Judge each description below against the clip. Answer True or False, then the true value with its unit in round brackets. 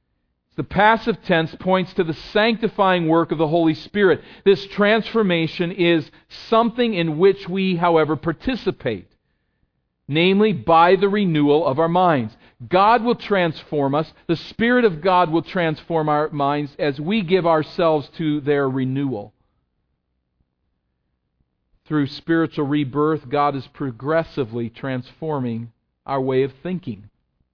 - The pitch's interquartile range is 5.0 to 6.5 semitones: True (5.6 semitones)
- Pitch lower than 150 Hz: False (160 Hz)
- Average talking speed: False (125 wpm)